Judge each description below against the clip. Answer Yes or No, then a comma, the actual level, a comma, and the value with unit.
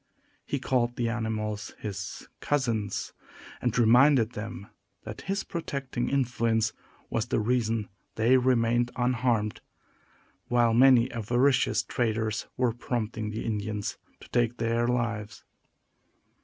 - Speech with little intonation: Yes, narrow, 2.1 semitones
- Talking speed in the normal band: No, slow, 115 wpm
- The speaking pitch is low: Yes, low, 120 Hz